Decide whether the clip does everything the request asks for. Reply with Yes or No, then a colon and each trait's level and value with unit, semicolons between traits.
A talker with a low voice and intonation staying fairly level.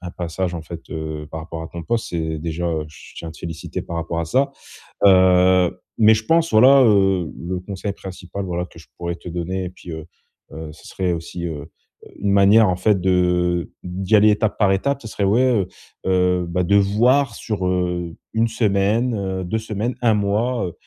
No: very low, 95 Hz; average, 3.5 semitones